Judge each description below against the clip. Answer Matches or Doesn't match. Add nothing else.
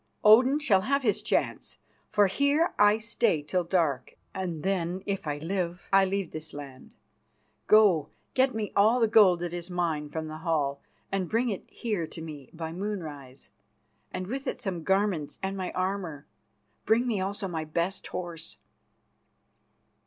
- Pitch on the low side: Doesn't match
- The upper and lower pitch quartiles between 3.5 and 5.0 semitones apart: Matches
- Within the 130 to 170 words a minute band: Matches